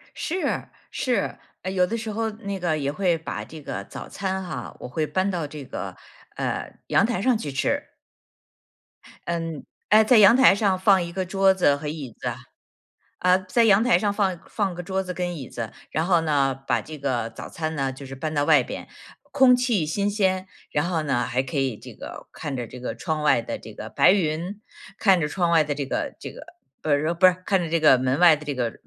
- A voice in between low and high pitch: Yes, medium, 170 Hz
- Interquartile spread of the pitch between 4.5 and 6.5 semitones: Yes, average, 5.0 semitones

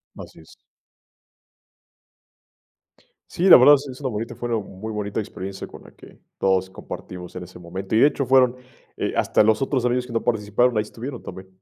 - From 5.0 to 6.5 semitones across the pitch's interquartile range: No, average, 4.6 semitones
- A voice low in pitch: Yes, low, 110 Hz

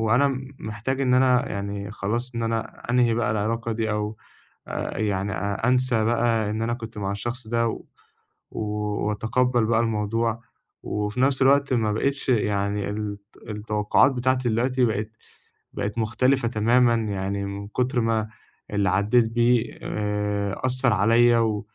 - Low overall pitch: Yes, low, 115 Hz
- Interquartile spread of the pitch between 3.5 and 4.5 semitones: No, average, 2.7 semitones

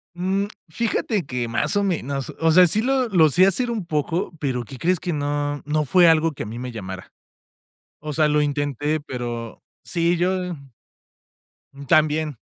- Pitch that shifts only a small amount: No, average, 4.3 semitones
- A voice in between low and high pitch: Yes, medium, 155 Hz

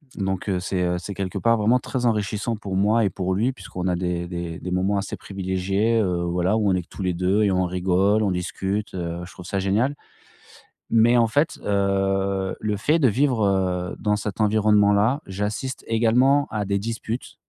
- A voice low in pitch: Yes, low, 100 Hz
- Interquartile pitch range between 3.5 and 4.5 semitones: No, average, 2.9 semitones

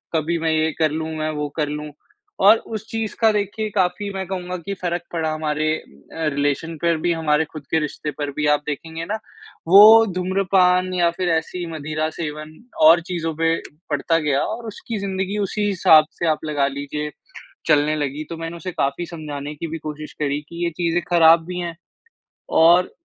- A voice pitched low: No, medium, 165 Hz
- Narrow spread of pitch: No, average, 3.0 semitones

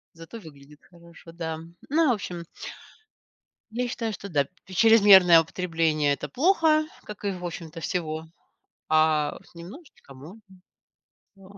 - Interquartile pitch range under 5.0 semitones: No, average, 5.3 semitones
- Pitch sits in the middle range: Yes, medium, 175 Hz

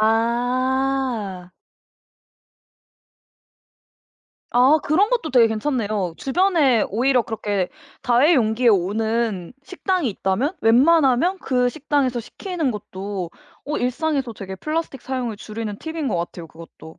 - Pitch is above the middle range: Yes, high, 245 Hz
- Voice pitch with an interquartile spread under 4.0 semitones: No, average, 5.2 semitones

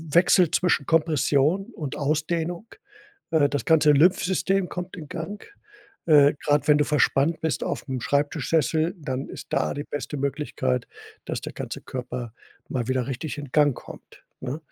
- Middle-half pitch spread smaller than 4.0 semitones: Yes, average, 2.9 semitones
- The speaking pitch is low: No, medium, 150 Hz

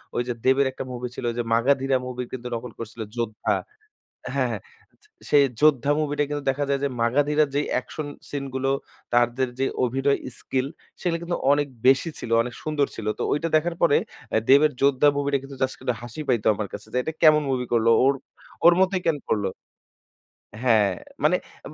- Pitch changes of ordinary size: Yes, average, 3.3 semitones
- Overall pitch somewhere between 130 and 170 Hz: Yes, low, 135 Hz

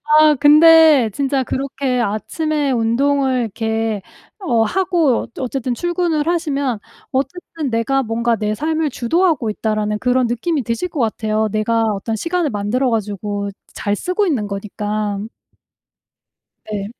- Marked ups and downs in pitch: Yes, wide, 5.7 semitones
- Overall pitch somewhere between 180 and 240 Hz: No, very high, 250 Hz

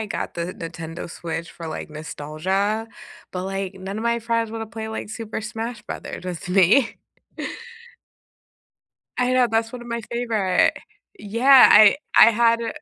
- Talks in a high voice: Yes, high, 215 Hz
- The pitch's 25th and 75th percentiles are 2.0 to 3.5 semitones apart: No, average, 4.0 semitones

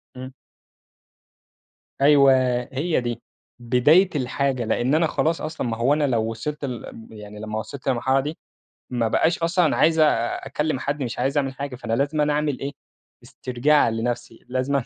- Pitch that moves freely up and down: No, average, 3.8 semitones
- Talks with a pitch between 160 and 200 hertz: No, low, 135 Hz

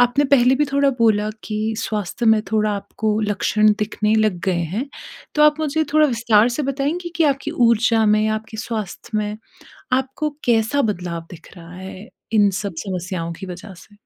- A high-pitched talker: Yes, high, 220 Hz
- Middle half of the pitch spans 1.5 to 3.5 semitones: No, average, 3.9 semitones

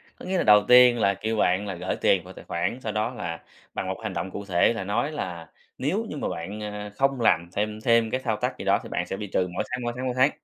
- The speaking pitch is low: Yes, low, 105 Hz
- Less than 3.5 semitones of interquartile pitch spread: No, average, 4.7 semitones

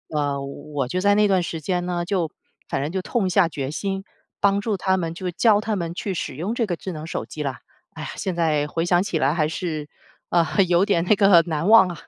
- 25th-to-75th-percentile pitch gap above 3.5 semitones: Yes, average, 3.9 semitones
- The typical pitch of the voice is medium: Yes, medium, 175 Hz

